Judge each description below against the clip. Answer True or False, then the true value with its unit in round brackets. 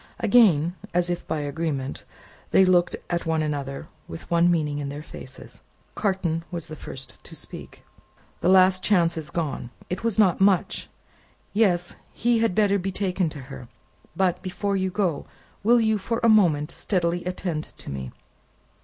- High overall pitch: False (175 Hz)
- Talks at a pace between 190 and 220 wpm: False (165 wpm)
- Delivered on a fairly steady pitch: False (4.0 semitones)